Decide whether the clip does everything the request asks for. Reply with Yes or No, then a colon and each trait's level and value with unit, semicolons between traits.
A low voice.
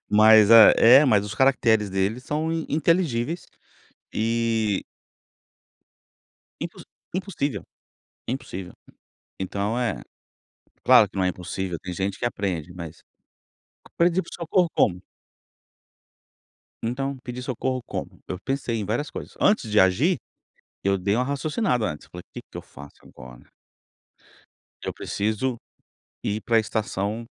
Yes: low, 110 Hz